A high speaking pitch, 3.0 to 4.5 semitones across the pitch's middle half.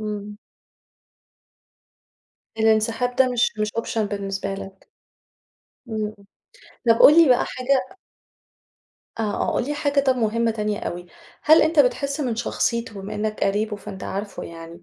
Yes: high, 220 Hz; average, 3.4 semitones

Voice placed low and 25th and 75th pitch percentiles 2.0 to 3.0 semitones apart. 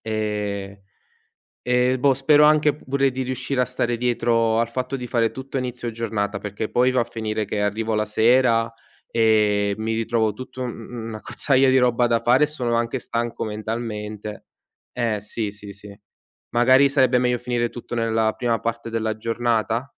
Yes: low, 115 Hz; narrow, 2.4 semitones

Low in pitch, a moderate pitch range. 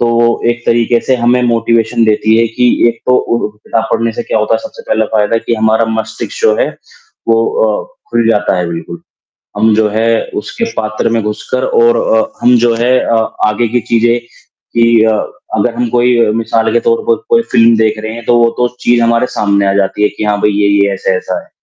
No: low, 115 Hz; narrow, 1.6 semitones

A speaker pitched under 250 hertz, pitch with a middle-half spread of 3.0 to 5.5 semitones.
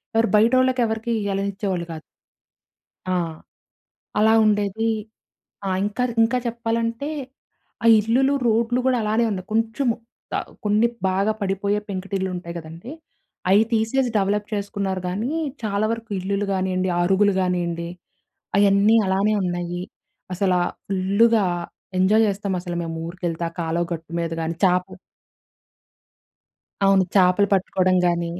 Yes: high, 200 Hz; average, 3.3 semitones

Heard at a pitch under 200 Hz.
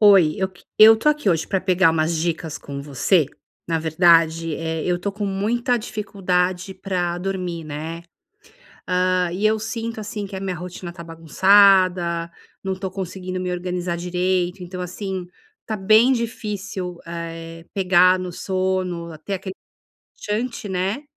Yes: medium, 185 Hz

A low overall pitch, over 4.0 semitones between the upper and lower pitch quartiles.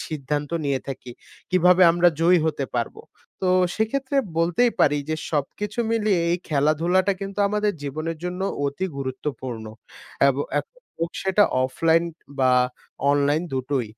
No: medium, 165 Hz; average, 5.0 semitones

